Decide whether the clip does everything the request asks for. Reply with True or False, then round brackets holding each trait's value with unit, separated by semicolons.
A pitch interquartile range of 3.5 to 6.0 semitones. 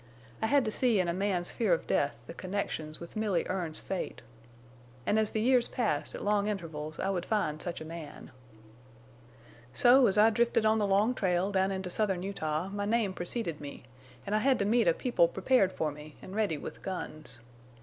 True (4.3 semitones)